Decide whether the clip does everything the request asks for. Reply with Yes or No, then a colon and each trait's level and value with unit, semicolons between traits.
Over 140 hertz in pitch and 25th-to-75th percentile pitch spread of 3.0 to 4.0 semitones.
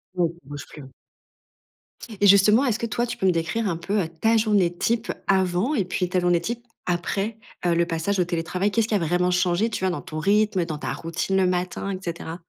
Yes: medium, 185 Hz; average, 3.4 semitones